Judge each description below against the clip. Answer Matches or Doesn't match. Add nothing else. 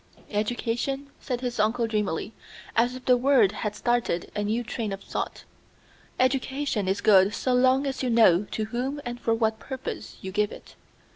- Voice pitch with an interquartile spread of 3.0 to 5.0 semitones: Matches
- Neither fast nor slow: Matches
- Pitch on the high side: Matches